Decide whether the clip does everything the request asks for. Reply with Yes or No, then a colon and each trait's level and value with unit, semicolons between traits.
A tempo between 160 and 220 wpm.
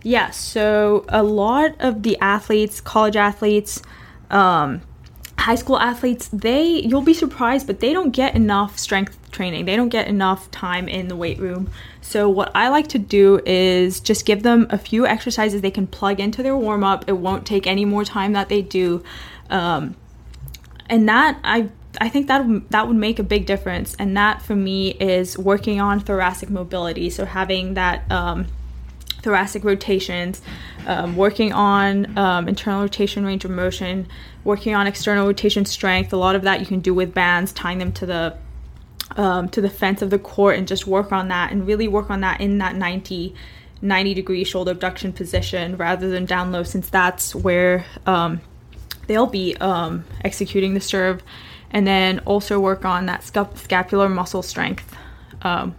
Yes: average, 175 wpm